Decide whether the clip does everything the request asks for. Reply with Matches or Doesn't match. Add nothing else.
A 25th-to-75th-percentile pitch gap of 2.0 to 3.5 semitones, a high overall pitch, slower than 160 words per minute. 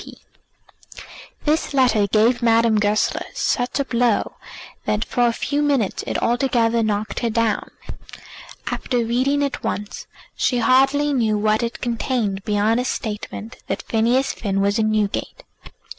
Matches